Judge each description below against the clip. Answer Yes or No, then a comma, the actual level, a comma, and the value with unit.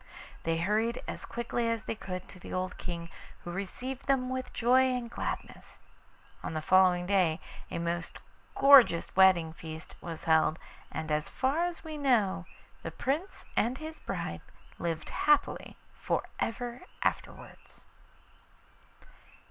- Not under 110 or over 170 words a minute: Yes, average, 140 wpm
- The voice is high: Yes, high, 200 Hz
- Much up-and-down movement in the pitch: Yes, wide, 7.1 semitones